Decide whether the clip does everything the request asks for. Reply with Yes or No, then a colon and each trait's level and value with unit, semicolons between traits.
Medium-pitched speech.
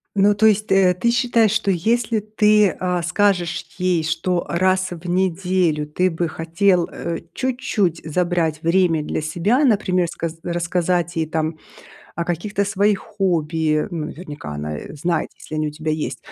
Yes: medium, 180 Hz